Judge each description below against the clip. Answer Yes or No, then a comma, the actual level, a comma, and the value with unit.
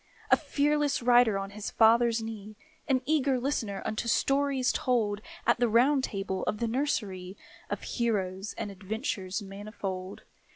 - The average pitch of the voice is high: Yes, high, 225 Hz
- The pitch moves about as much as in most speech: Yes, average, 4.3 semitones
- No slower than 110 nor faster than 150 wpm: Yes, average, 140 wpm